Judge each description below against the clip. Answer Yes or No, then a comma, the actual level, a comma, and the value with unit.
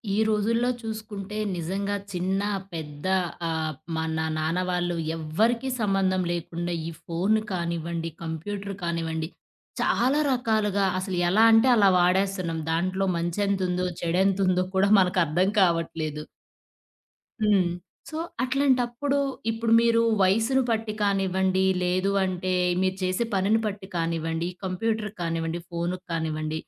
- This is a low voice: No, medium, 185 Hz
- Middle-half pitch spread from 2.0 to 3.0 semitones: No, average, 3.7 semitones